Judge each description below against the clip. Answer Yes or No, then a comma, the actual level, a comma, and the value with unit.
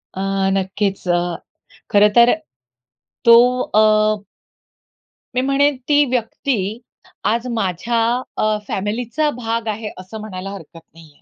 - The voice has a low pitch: No, high, 215 Hz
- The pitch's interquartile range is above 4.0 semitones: No, average, 3.4 semitones